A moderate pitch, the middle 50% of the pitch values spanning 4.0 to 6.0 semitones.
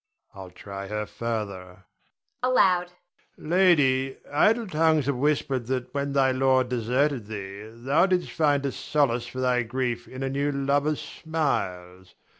No: low, 130 Hz; average, 4.4 semitones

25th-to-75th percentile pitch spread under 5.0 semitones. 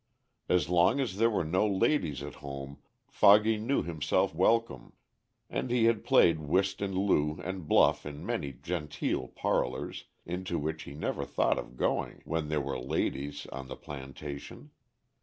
No: wide, 5.6 semitones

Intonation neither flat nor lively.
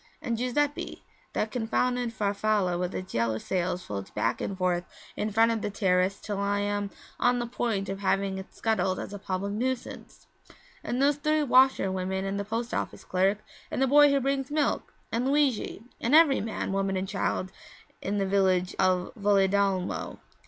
Yes: average, 4.2 semitones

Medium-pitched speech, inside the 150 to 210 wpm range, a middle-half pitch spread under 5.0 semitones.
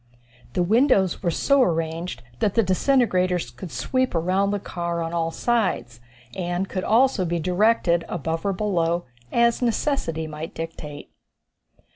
No: medium, 180 Hz; average, 140 wpm; average, 4.6 semitones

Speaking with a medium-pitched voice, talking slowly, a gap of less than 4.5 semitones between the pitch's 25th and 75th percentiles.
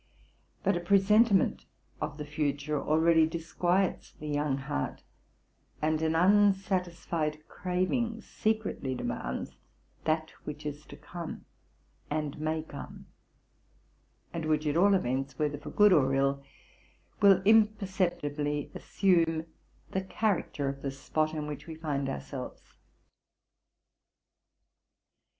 Yes: medium, 160 Hz; slow, 115 wpm; average, 4.1 semitones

